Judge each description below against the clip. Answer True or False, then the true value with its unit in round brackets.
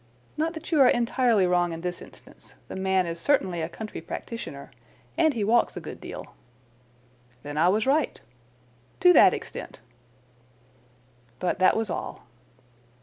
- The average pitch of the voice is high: True (205 Hz)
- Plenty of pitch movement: True (6.5 semitones)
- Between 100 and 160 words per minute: True (150 wpm)